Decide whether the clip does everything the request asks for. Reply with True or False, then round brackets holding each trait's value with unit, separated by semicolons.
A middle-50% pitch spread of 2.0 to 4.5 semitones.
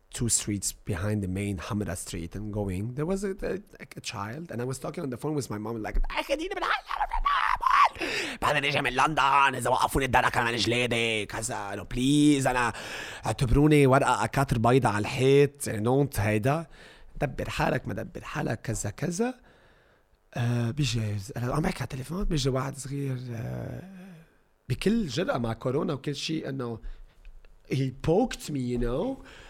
False (5.1 semitones)